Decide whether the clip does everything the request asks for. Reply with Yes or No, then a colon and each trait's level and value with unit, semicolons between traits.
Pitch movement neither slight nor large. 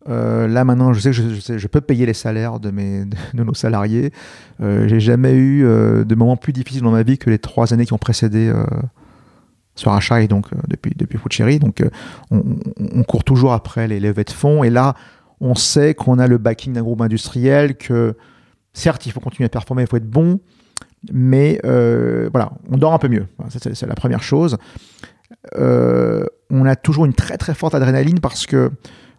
Yes: average, 3.1 semitones